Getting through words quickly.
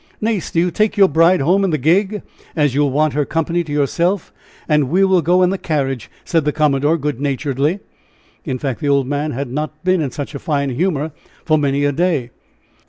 Yes: fast, 220 wpm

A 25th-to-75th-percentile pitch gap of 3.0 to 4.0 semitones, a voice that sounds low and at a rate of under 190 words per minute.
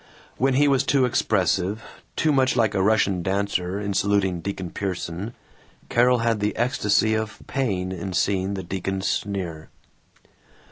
Yes: average, 3.7 semitones; low, 100 Hz; average, 145 wpm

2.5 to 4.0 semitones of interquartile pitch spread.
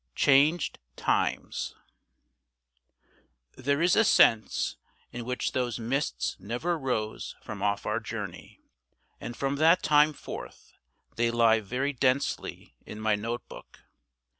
No: average, 4.4 semitones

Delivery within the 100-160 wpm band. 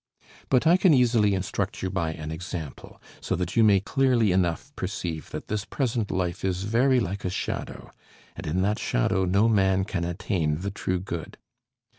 No: average, 180 wpm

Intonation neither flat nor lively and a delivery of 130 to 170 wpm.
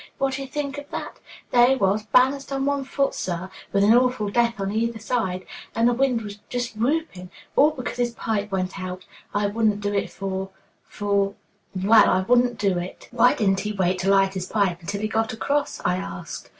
No: average, 4.2 semitones; fast, 205 wpm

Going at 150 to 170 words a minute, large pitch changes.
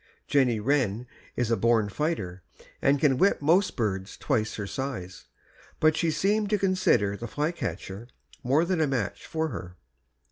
Yes: average, 155 wpm; wide, 7.3 semitones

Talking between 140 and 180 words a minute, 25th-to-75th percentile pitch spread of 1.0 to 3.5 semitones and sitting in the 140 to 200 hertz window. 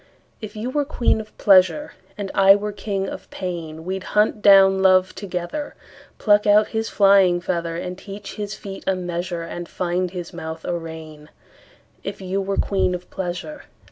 Yes: average, 145 wpm; narrow, 2.6 semitones; high, 190 Hz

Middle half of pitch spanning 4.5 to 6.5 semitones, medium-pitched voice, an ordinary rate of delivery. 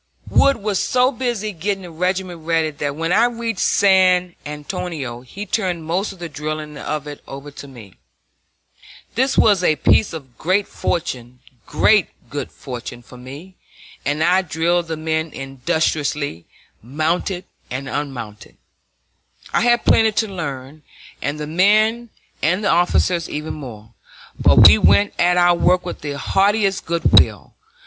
Yes: average, 4.9 semitones; medium, 165 Hz; average, 145 wpm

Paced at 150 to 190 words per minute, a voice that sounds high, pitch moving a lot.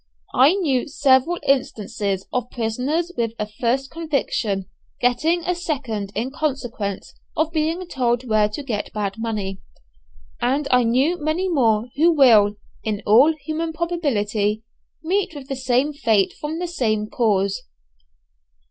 No: average, 140 wpm; very high, 255 Hz; wide, 6.2 semitones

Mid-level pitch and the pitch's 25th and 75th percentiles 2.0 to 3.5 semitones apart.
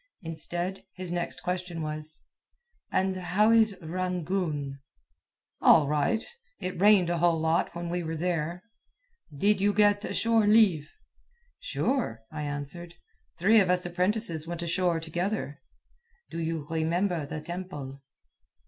Yes: medium, 175 Hz; average, 3.1 semitones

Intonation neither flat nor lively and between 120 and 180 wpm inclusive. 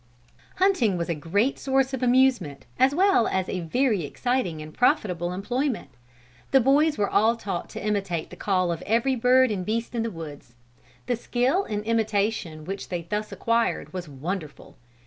No: wide, 6.1 semitones; average, 170 wpm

